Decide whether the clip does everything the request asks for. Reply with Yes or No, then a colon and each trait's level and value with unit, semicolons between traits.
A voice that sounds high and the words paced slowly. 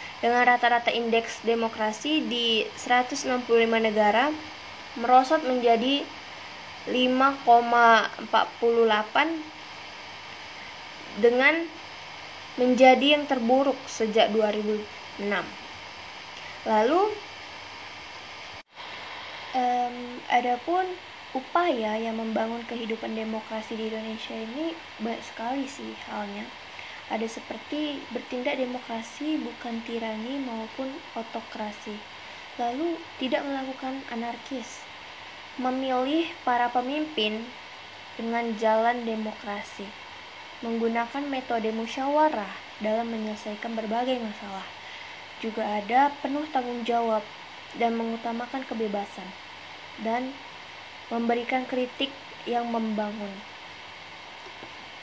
Yes: high, 240 Hz; slow, 75 wpm